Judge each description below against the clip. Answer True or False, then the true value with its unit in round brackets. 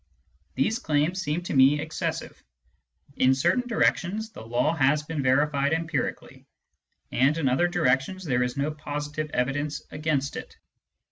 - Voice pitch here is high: False (150 Hz)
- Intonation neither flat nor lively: True (3.3 semitones)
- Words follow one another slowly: False (145 wpm)